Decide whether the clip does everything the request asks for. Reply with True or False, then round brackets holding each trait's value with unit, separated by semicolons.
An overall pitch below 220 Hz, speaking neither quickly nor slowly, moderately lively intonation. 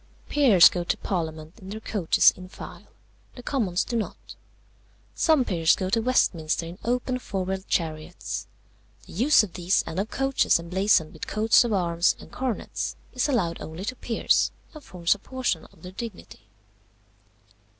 False (190 Hz; 165 wpm; 5.8 semitones)